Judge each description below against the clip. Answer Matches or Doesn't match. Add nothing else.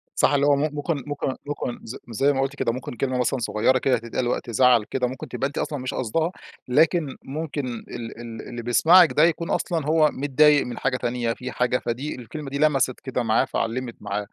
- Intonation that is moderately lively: Matches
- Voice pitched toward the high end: Doesn't match